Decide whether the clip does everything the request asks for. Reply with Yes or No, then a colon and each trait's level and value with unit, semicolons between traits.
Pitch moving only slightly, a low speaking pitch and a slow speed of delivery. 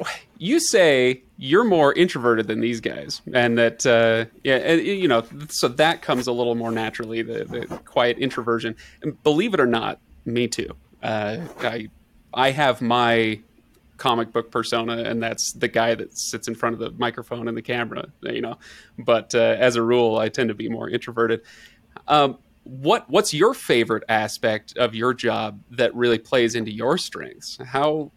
No: narrow, 1.7 semitones; low, 115 Hz; average, 175 wpm